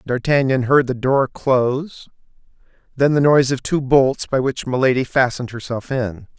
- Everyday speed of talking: Yes, average, 160 wpm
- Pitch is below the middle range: Yes, low, 130 Hz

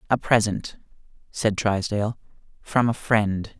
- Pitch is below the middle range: Yes, low, 105 Hz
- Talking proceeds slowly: Yes, slow, 115 wpm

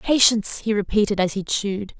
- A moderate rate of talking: Yes, average, 180 wpm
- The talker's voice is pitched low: No, high, 205 Hz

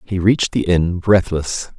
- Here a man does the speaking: Yes, male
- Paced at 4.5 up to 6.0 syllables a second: No, 4.3 syllables/s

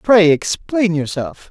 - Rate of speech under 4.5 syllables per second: Yes, 3.6 syllables/s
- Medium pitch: Yes, medium, 180 Hz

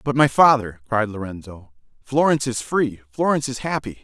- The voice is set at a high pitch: No, low, 120 Hz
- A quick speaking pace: No, average, 165 wpm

